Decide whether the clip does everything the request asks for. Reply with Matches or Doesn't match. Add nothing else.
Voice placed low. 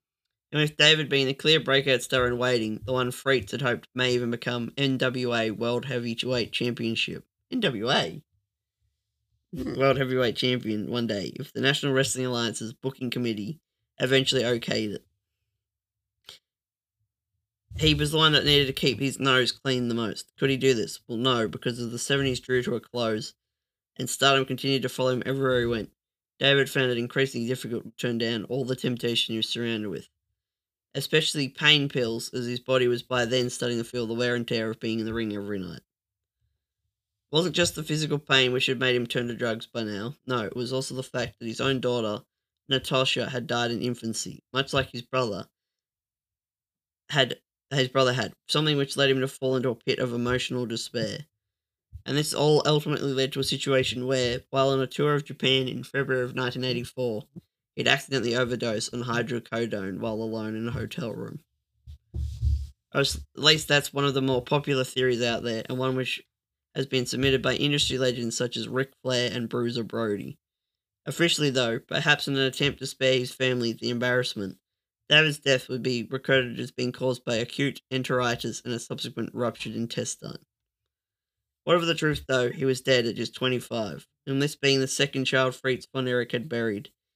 Matches